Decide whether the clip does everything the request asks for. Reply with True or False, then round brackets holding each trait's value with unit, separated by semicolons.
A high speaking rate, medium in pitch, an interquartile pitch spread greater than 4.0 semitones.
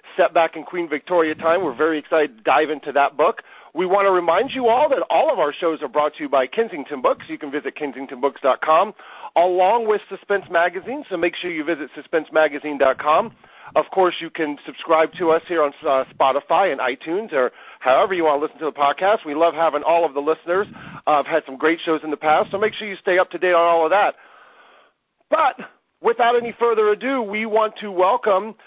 True (220 wpm; 165 Hz; 4.4 semitones)